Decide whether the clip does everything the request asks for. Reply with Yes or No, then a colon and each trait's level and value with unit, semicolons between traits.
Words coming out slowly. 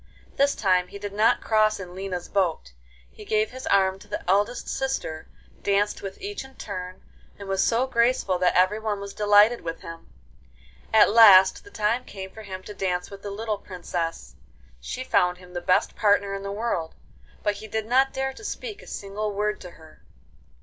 No: average, 190 wpm